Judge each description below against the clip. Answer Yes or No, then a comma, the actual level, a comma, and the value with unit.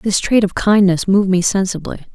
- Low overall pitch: No, high, 190 Hz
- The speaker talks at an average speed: Yes, average, 195 wpm